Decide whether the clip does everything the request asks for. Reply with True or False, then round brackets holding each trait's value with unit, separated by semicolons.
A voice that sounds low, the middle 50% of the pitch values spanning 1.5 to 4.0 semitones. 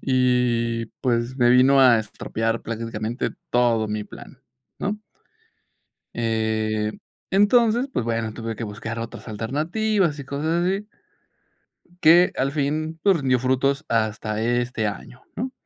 False (125 Hz; 5.2 semitones)